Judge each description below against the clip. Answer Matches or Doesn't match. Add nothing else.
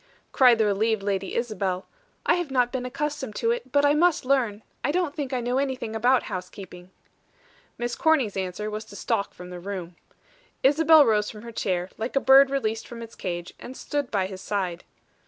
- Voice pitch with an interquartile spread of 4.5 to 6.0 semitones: Matches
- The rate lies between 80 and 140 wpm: Doesn't match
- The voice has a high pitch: Matches